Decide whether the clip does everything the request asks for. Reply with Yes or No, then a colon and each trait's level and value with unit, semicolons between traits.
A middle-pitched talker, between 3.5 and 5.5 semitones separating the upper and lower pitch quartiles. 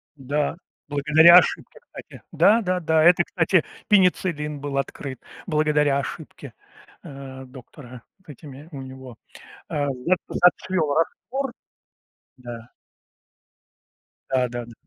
Yes: medium, 145 Hz; average, 4.1 semitones